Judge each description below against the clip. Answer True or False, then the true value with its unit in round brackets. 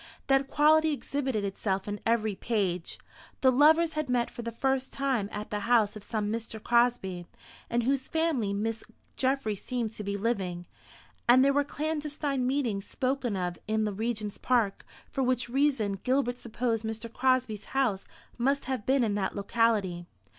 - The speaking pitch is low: False (235 Hz)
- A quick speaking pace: False (165 wpm)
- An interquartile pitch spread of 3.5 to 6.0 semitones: True (4.4 semitones)